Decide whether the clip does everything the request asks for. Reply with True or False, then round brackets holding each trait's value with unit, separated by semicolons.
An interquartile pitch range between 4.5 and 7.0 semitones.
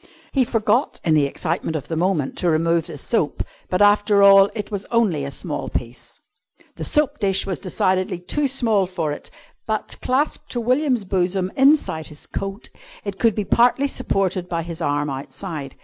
True (5.4 semitones)